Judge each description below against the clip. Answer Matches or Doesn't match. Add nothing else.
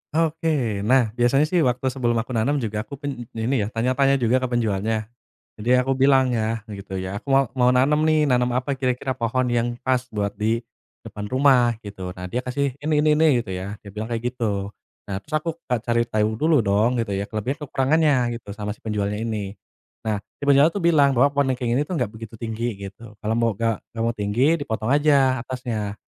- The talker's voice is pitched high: Doesn't match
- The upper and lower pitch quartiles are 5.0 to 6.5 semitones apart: Doesn't match